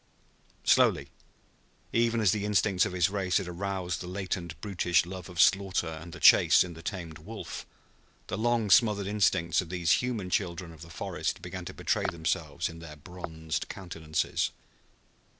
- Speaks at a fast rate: No, average, 165 wpm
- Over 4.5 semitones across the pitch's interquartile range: No, average, 3.2 semitones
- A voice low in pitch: Yes, very low, 90 Hz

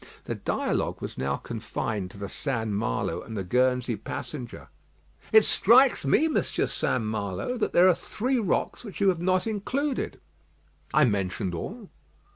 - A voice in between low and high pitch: No, low, 130 Hz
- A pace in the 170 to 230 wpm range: No, average, 155 wpm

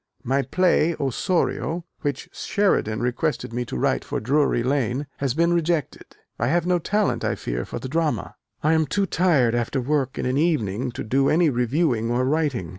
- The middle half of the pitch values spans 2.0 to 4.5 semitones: No, average, 5.2 semitones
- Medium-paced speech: Yes, average, 185 wpm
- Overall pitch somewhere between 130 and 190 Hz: Yes, medium, 140 Hz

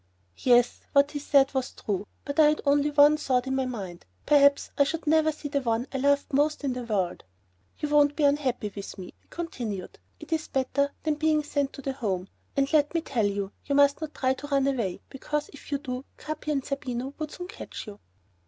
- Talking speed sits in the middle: No, fast, 225 wpm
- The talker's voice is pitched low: No, very high, 280 Hz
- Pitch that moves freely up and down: No, average, 2.9 semitones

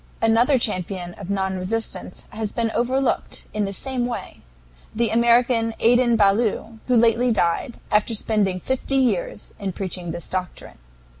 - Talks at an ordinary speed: Yes, average, 145 wpm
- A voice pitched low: No, high, 225 Hz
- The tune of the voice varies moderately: Yes, average, 3.5 semitones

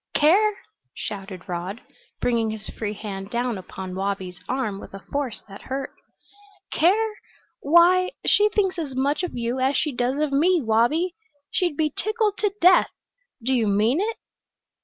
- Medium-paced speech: Yes, average, 160 wpm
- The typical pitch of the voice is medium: No, very high, 265 Hz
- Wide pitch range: Yes, wide, 8.7 semitones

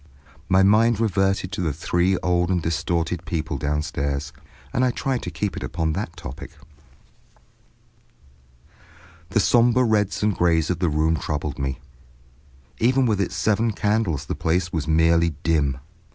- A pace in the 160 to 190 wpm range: No, average, 150 wpm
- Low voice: Yes, very low, 90 Hz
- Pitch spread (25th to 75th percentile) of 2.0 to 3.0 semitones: No, average, 4.6 semitones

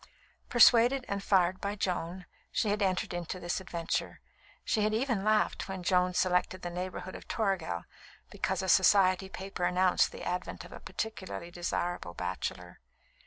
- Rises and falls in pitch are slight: Yes, narrow, 2.2 semitones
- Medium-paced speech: Yes, average, 155 wpm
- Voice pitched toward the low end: No, medium, 185 Hz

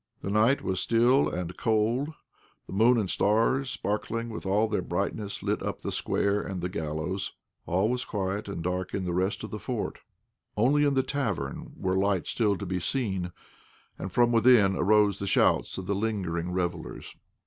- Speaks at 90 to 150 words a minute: No, average, 180 wpm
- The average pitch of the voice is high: No, low, 100 Hz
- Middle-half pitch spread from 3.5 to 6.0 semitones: Yes, average, 3.8 semitones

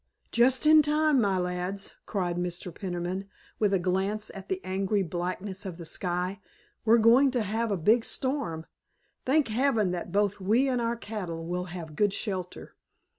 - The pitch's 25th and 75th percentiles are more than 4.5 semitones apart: No, average, 4.2 semitones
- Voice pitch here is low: No, high, 195 Hz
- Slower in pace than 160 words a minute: No, average, 170 wpm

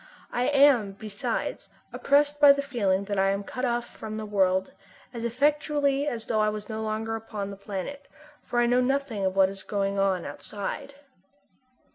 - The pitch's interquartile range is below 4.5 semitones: No, wide, 5.5 semitones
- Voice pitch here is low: No, high, 220 Hz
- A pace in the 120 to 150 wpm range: No, average, 180 wpm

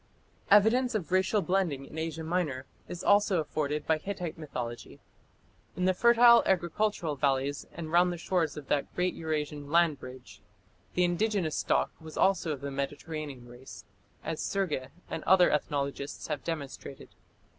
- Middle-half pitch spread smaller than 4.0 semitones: No, average, 4.3 semitones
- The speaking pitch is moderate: Yes, medium, 160 Hz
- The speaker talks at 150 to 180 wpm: Yes, average, 155 wpm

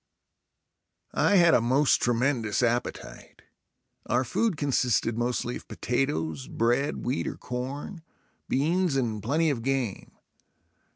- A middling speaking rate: No, slow, 115 wpm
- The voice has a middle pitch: No, low, 125 Hz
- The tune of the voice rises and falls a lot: No, average, 3.5 semitones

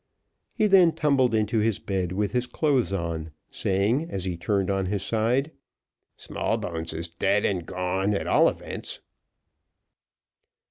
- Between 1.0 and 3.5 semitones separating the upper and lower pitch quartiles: No, average, 5.0 semitones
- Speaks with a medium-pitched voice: No, low, 100 Hz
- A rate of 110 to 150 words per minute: Yes, average, 140 wpm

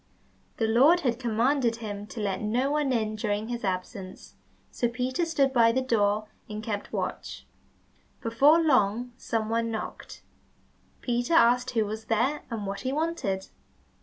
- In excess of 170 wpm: No, average, 155 wpm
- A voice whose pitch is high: Yes, high, 230 Hz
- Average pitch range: Yes, average, 3.3 semitones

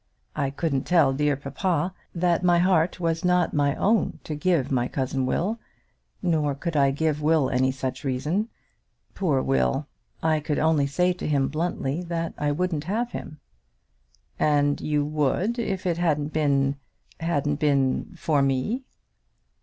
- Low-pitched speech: No, medium, 150 Hz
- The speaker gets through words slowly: No, average, 155 wpm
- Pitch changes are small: No, average, 3.9 semitones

